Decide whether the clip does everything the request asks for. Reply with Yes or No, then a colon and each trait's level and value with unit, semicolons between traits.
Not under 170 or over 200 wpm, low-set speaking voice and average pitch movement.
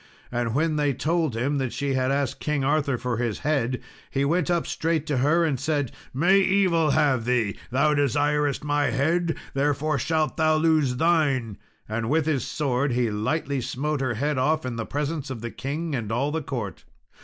No: average, 190 wpm; medium, 145 Hz; average, 3.6 semitones